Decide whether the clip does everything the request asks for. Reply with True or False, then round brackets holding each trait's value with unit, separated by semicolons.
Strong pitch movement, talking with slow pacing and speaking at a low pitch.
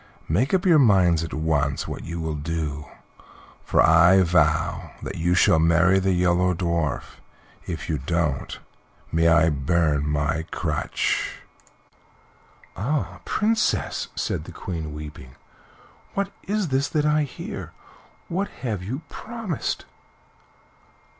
True (6.4 semitones; 125 wpm; 85 Hz)